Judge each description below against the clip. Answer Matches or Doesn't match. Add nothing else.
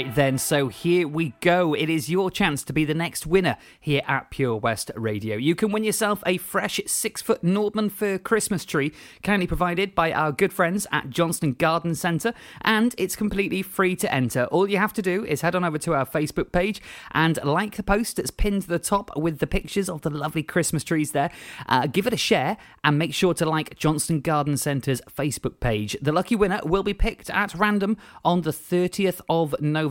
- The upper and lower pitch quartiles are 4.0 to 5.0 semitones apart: Matches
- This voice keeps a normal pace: Doesn't match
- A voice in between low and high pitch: Matches